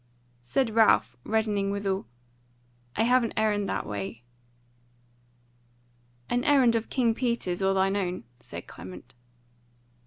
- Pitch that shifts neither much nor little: Yes, average, 3.3 semitones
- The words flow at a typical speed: No, slow, 120 wpm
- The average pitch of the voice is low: No, high, 205 Hz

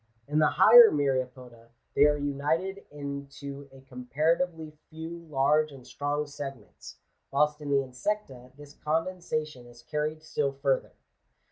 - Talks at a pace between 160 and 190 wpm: No, slow, 135 wpm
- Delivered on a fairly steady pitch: Yes, narrow, 2.3 semitones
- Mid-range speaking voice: Yes, medium, 145 Hz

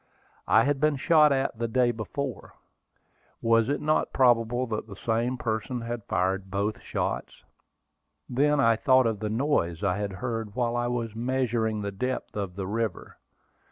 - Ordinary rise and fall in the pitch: Yes, average, 3.3 semitones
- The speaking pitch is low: Yes, low, 115 Hz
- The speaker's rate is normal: Yes, average, 165 wpm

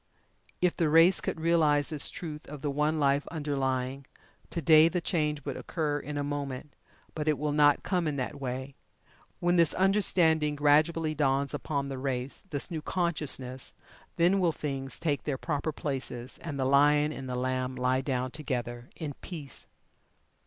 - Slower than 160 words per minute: No, average, 170 wpm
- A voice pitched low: No, medium, 145 Hz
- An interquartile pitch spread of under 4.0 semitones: Yes, average, 2.8 semitones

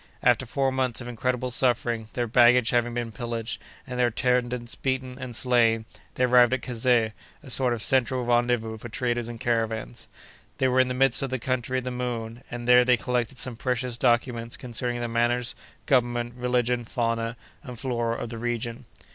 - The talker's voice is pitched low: Yes, low, 120 Hz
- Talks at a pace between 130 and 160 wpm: No, average, 185 wpm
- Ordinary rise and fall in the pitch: No, narrow, 1.3 semitones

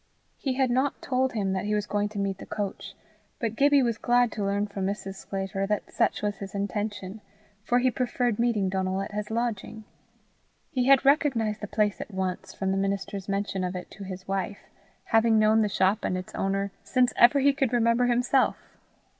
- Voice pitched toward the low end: No, high, 210 Hz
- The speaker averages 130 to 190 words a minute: No, average, 200 wpm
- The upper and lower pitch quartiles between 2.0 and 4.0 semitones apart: Yes, average, 3.6 semitones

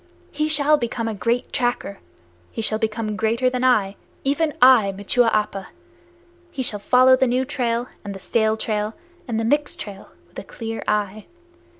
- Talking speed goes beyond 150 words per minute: Yes, average, 175 wpm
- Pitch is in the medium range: No, high, 230 Hz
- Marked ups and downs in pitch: No, average, 3.1 semitones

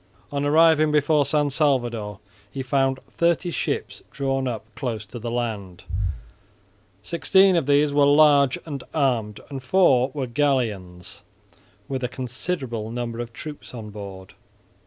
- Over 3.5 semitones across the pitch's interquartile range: Yes, average, 4.1 semitones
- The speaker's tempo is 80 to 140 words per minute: Yes, slow, 135 wpm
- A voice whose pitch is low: Yes, low, 130 Hz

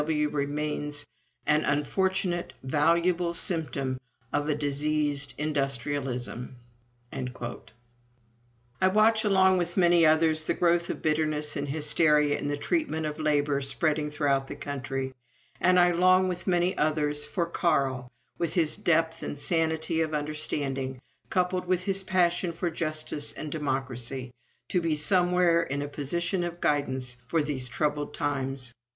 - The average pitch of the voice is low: No, medium, 150 Hz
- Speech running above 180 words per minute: No, slow, 135 wpm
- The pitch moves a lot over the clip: No, average, 3.6 semitones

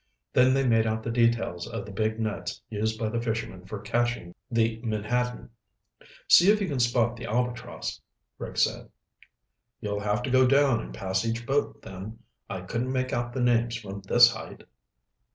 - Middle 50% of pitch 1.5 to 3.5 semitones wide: Yes, narrow, 2.5 semitones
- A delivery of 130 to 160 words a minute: No, average, 180 wpm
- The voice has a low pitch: Yes, low, 115 Hz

